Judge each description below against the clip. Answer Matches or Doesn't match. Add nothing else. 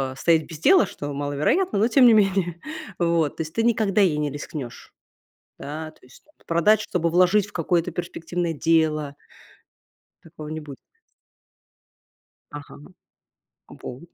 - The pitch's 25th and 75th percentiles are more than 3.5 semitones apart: Matches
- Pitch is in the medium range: Matches